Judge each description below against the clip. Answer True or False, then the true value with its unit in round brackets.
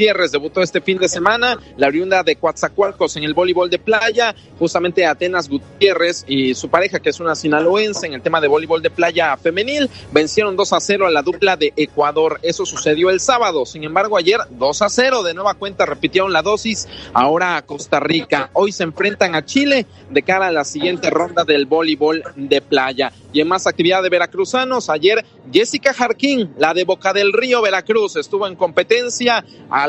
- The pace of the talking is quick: True (195 wpm)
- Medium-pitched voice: True (180 Hz)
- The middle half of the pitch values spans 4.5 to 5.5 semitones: True (5.1 semitones)